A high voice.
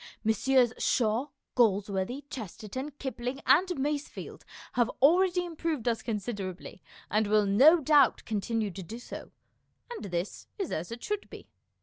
Yes: high, 240 Hz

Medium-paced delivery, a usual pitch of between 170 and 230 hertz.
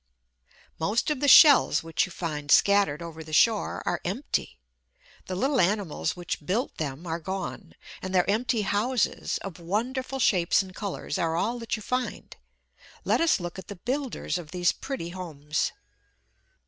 Yes: average, 160 wpm; high, 190 Hz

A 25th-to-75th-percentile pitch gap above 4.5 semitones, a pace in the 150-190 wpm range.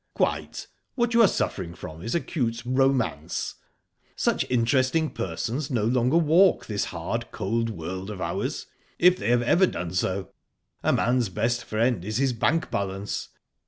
Yes: wide, 5.6 semitones; average, 155 wpm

